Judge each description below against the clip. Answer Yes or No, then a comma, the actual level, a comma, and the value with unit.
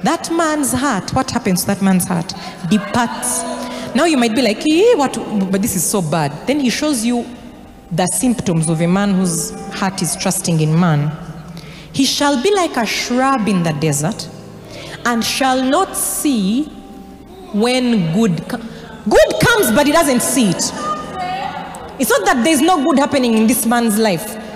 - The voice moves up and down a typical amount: No, wide, 6.3 semitones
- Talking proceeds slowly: No, average, 175 wpm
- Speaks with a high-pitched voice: Yes, high, 225 Hz